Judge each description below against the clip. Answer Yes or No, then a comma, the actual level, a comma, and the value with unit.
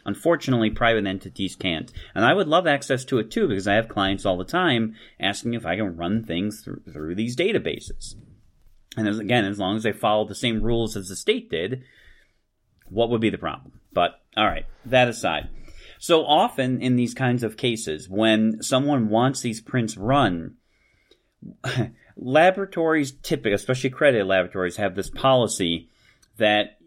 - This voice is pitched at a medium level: No, low, 110 Hz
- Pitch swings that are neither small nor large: Yes, average, 4.2 semitones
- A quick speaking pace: No, average, 170 wpm